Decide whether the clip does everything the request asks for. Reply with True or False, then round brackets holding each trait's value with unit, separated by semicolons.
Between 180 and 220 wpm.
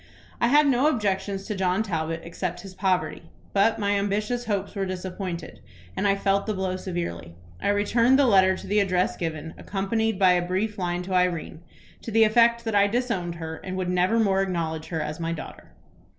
True (195 wpm)